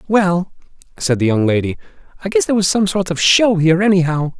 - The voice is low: No, medium, 175 Hz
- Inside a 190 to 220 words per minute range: Yes, fast, 205 wpm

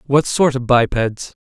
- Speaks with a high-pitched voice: No, low, 130 Hz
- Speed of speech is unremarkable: Yes, average, 165 wpm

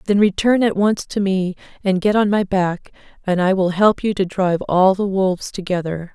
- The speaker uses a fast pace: Yes, fast, 215 wpm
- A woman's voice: Yes, female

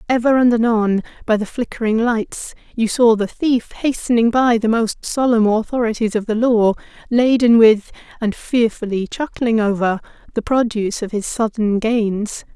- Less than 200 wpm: Yes, average, 155 wpm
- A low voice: No, high, 225 Hz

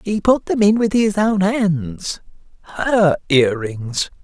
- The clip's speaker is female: No, male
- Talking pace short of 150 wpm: No, average, 155 wpm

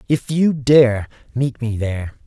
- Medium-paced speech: Yes, average, 160 wpm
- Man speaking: Yes, male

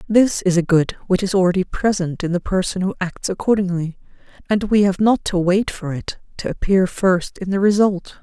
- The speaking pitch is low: No, high, 190 Hz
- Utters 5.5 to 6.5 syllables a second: No, 5.1 syllables/s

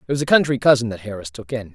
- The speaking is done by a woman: No, male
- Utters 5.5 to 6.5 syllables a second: No, 7.0 syllables/s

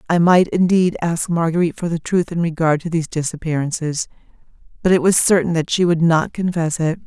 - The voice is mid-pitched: Yes, medium, 165 Hz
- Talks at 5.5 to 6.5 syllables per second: Yes, 5.7 syllables/s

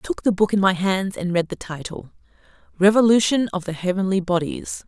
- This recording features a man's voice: No, female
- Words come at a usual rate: Yes, average, 195 wpm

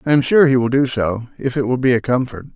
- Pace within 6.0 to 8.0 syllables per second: Yes, 6.2 syllables/s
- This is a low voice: Yes, low, 125 Hz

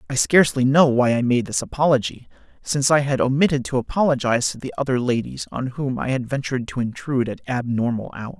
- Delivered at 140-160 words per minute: No, average, 200 wpm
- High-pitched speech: No, low, 130 Hz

